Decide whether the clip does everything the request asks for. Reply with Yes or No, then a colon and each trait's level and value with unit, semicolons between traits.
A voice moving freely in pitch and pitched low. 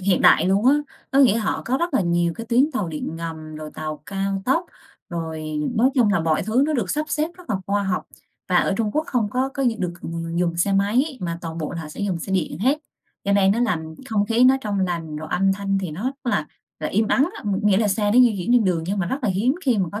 No: wide, 5.9 semitones; high, 200 Hz